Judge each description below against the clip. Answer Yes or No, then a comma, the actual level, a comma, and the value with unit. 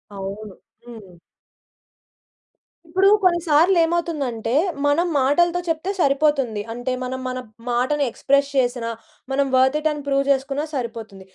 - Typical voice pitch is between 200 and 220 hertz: No, very high, 275 Hz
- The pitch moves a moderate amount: Yes, average, 4.2 semitones